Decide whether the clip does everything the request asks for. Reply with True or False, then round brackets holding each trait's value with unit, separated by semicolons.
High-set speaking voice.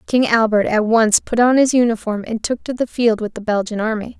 True (225 Hz)